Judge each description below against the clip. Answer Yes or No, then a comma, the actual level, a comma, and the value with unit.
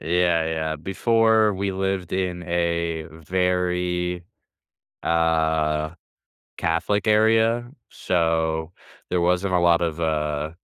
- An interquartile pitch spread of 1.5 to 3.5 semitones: Yes, narrow, 2.5 semitones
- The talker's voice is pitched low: Yes, very low, 85 Hz